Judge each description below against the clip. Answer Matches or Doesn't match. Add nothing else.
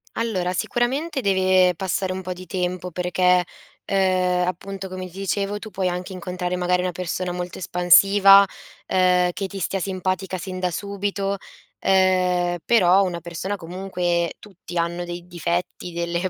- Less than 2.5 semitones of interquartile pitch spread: Matches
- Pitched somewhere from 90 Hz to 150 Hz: Doesn't match